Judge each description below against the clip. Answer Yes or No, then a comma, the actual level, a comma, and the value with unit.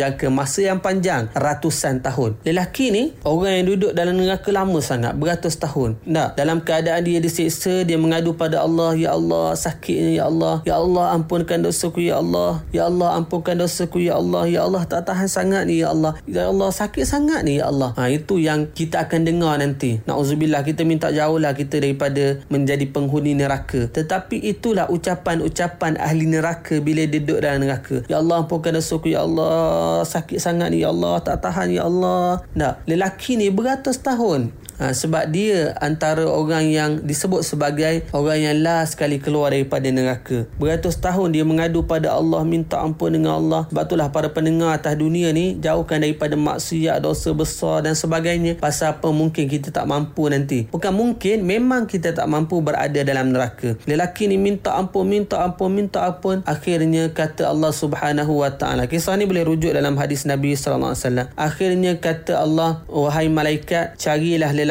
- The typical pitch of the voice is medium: Yes, medium, 160 Hz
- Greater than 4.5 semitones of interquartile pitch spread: No, average, 3.2 semitones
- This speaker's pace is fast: Yes, fast, 180 wpm